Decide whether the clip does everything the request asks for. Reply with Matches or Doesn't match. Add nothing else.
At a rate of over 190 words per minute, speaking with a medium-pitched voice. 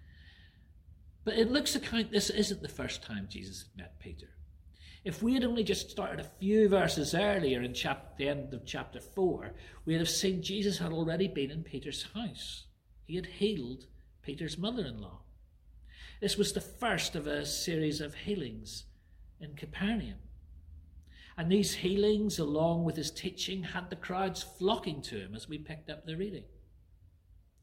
Doesn't match